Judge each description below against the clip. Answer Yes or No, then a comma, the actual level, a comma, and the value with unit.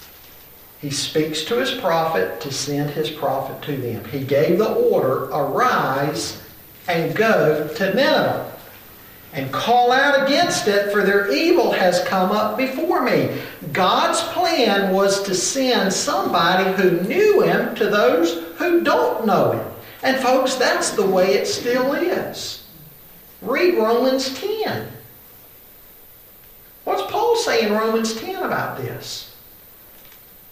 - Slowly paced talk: Yes, slow, 130 wpm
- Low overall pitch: No, high, 205 Hz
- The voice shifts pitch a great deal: Yes, wide, 8.7 semitones